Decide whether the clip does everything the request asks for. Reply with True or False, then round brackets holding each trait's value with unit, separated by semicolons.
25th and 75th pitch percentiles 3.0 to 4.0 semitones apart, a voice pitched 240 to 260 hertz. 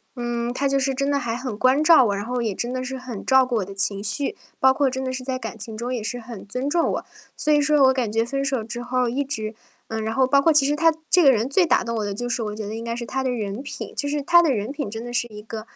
True (3.5 semitones; 250 Hz)